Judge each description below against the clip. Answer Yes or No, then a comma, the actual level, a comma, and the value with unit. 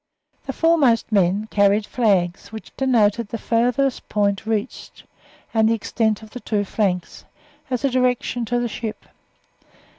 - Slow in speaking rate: No, average, 145 wpm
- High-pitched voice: Yes, high, 225 Hz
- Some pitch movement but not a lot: Yes, average, 3.1 semitones